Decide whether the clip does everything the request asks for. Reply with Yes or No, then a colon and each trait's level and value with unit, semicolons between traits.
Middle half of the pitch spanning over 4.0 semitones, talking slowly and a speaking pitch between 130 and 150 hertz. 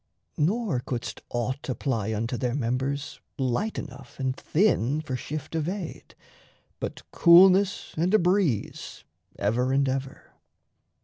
Yes: average, 5.2 semitones; slow, 125 wpm; medium, 140 Hz